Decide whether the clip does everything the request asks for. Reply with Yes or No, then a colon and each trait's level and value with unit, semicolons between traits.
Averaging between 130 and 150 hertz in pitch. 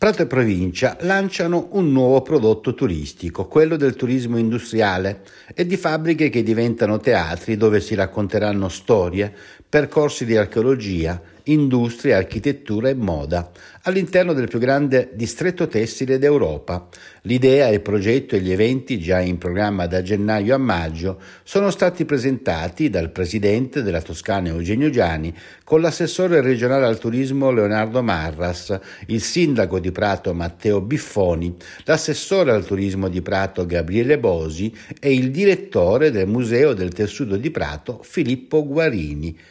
No: low, 115 Hz